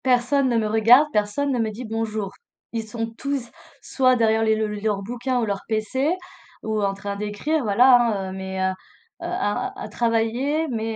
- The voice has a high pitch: Yes, high, 225 Hz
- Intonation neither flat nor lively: Yes, average, 3.3 semitones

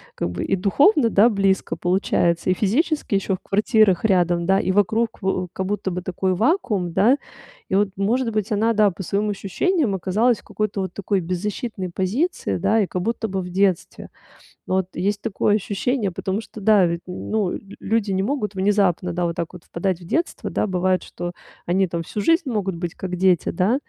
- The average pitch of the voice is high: Yes, high, 195 Hz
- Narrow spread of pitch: No, average, 3.0 semitones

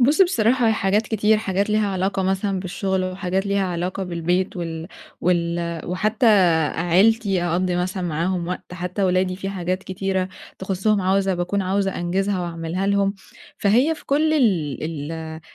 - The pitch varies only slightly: Yes, narrow, 2.2 semitones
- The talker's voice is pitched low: No, high, 190 Hz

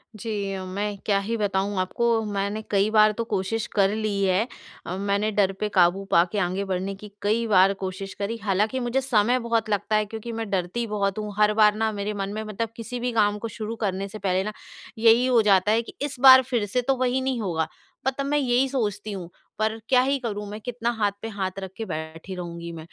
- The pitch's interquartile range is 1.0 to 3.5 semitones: Yes, average, 2.7 semitones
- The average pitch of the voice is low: No, high, 210 Hz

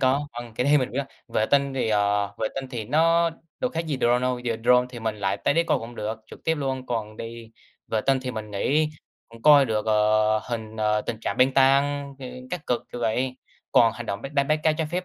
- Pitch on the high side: No, low, 125 Hz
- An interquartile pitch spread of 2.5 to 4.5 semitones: Yes, average, 4.2 semitones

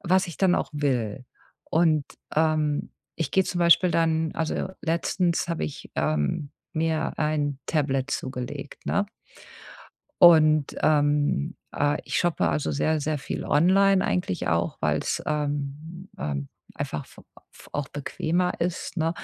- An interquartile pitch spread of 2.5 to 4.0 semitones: Yes, average, 2.9 semitones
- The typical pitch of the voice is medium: Yes, medium, 155 Hz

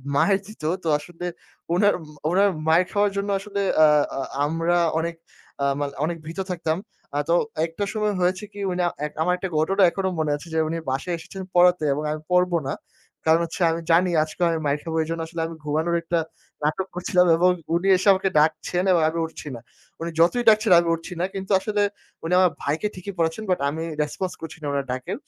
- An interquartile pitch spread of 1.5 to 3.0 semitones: Yes, average, 2.7 semitones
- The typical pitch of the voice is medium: Yes, medium, 170 Hz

